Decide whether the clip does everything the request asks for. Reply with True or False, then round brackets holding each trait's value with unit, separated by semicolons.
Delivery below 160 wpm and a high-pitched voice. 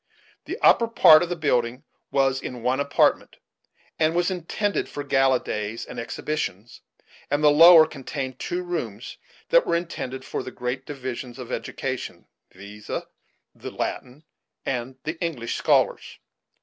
False (145 wpm; 135 Hz)